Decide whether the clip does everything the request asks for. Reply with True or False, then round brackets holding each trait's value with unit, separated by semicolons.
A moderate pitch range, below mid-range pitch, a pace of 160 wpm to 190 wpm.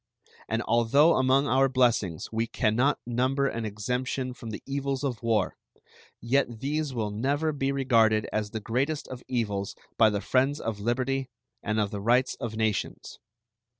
True (3.7 semitones; 120 Hz; 165 wpm)